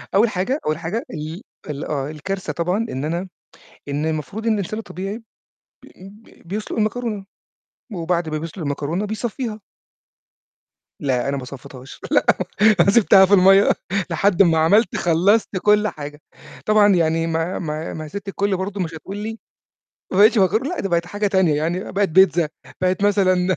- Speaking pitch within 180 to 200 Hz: Yes, medium, 185 Hz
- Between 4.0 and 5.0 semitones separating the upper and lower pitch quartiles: Yes, average, 4.3 semitones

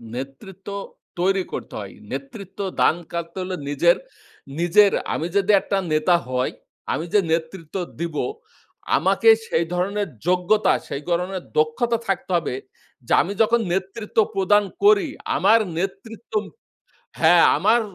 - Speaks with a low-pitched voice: No, high, 190 Hz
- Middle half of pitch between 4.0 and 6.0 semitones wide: No, average, 3.6 semitones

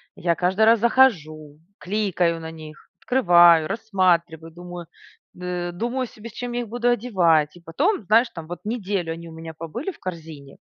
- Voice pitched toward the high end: No, medium, 180 Hz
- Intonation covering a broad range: Yes, wide, 5.7 semitones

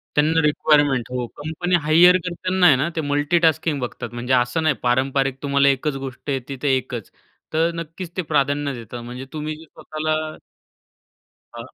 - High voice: No, medium, 145 Hz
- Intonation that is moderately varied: Yes, average, 3.3 semitones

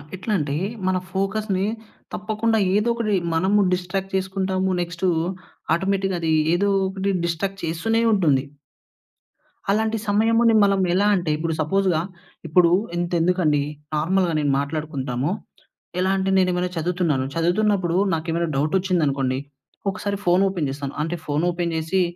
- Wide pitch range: No, average, 3.3 semitones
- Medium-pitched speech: Yes, medium, 180 Hz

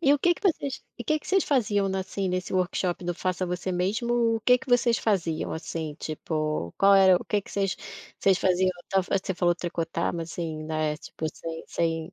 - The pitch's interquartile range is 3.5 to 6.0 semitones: Yes, average, 4.0 semitones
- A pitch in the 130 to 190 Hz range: Yes, medium, 185 Hz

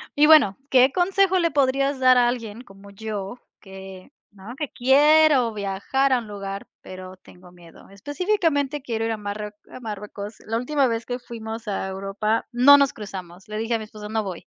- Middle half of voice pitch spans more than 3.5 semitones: Yes, average, 5.2 semitones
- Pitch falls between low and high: No, high, 225 Hz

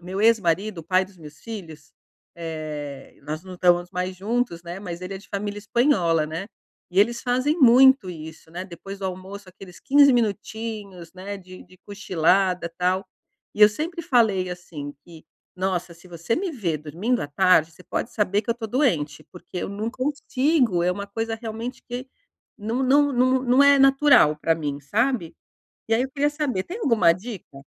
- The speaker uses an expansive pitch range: Yes, wide, 5.7 semitones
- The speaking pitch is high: Yes, high, 195 Hz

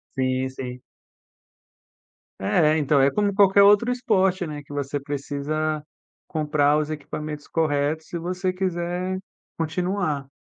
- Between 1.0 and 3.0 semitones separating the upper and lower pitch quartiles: No, average, 4.2 semitones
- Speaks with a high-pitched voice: No, medium, 155 Hz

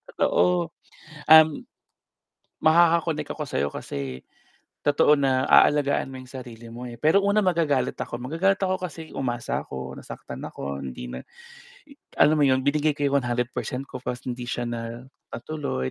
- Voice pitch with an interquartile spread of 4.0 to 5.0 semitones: Yes, average, 4.7 semitones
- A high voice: No, low, 135 Hz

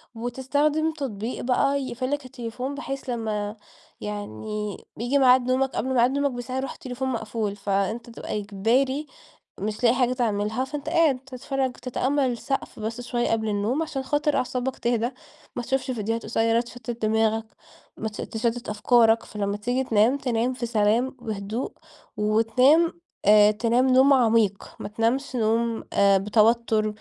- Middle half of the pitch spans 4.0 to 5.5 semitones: No, average, 3.3 semitones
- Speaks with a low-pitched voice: No, high, 240 Hz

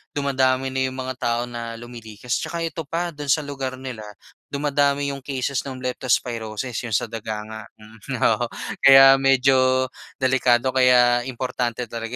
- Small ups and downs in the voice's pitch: Yes, narrow, 2.1 semitones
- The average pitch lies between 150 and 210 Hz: No, low, 130 Hz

